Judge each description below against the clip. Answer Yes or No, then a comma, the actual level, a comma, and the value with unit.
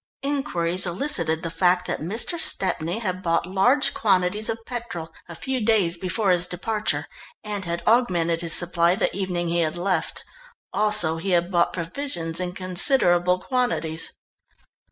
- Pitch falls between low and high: Yes, medium, 180 Hz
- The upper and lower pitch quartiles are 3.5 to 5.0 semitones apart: Yes, average, 3.8 semitones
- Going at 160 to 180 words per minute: No, average, 150 wpm